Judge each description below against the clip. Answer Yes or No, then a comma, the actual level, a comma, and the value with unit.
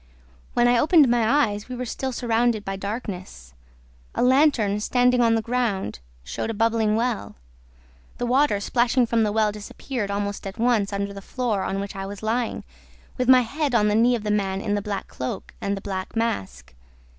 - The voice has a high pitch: Yes, high, 220 Hz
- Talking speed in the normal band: Yes, average, 195 wpm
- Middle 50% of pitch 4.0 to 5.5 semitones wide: No, average, 3.4 semitones